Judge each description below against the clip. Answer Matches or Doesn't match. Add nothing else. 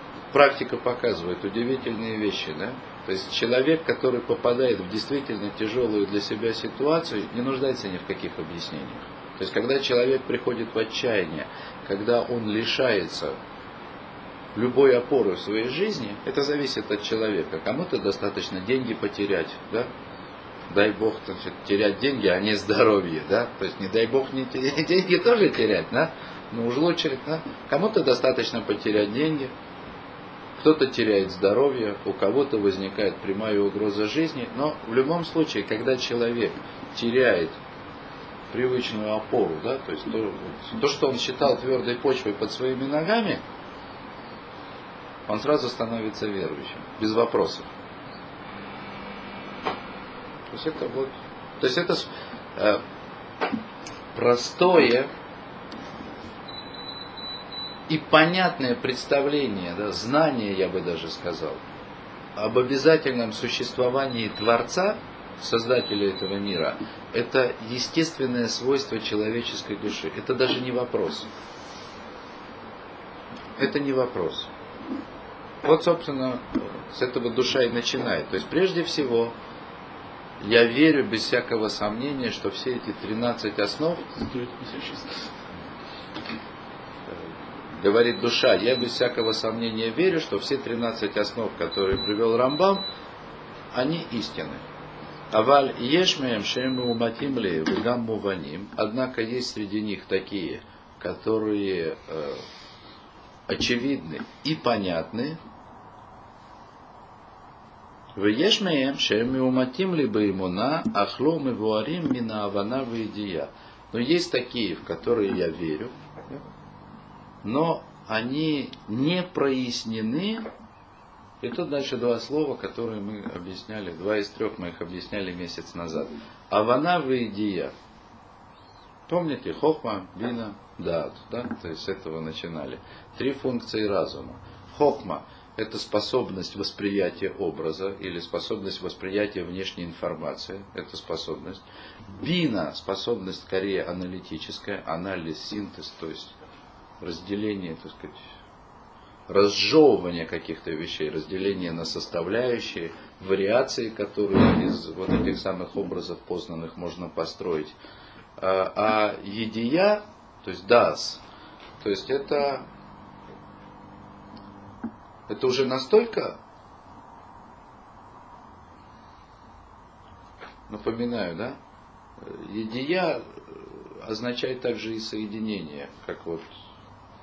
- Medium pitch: Doesn't match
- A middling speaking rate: Doesn't match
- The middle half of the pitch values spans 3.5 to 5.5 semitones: Matches